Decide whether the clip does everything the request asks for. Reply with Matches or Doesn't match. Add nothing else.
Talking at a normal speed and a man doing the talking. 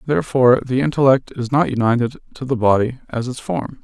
Matches